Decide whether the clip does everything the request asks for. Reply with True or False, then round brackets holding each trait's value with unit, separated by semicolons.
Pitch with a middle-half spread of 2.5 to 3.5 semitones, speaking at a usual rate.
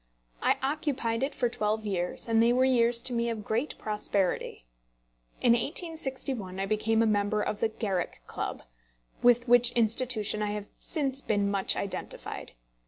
True (3.0 semitones; 160 wpm)